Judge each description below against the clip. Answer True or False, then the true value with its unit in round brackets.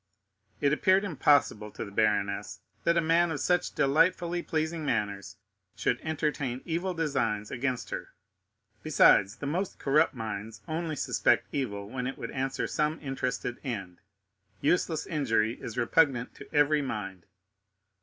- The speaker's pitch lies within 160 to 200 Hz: False (135 Hz)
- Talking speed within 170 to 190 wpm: False (135 wpm)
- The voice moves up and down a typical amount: False (6.6 semitones)